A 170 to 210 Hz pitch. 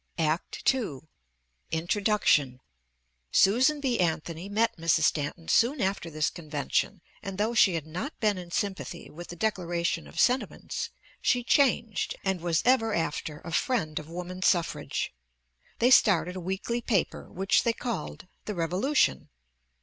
Yes: medium, 185 Hz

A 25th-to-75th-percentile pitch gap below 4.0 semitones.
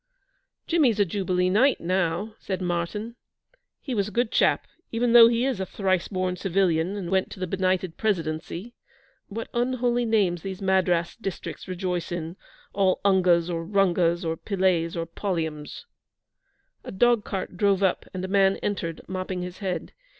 Yes: average, 2.9 semitones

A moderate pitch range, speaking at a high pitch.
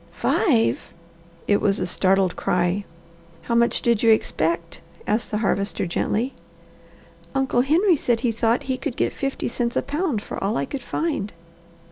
Yes: average, 4.7 semitones; high, 225 Hz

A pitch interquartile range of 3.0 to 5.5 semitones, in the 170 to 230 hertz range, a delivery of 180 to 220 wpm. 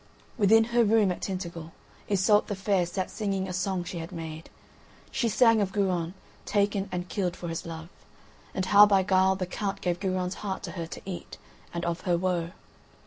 No: narrow, 2.5 semitones; high, 190 Hz; average, 195 wpm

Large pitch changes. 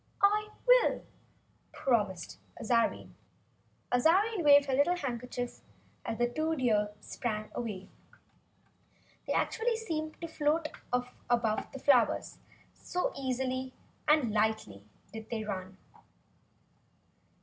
Yes: wide, 5.9 semitones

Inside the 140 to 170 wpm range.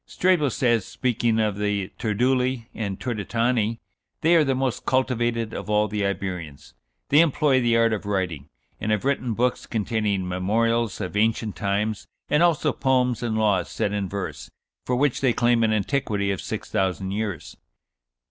Yes: average, 165 wpm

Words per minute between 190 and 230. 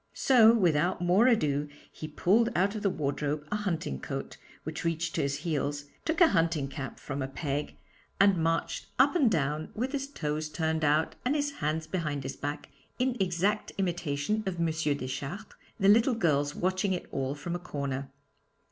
No: average, 180 wpm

